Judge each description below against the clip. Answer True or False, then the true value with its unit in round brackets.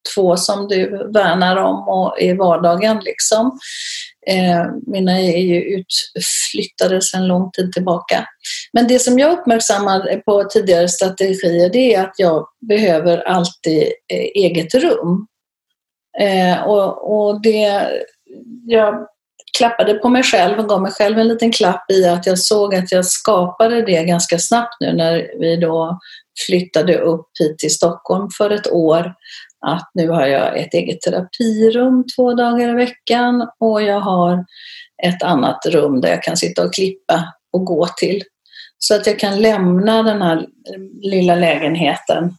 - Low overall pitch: False (190 Hz)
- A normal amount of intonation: True (4.4 semitones)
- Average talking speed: True (155 wpm)